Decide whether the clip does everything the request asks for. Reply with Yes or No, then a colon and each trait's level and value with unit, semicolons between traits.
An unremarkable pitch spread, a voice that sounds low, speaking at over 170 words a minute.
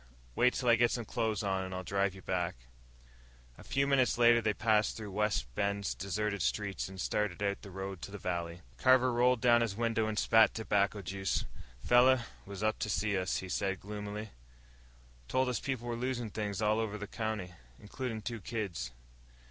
Yes: average, 3.1 semitones; low, 105 Hz; average, 190 wpm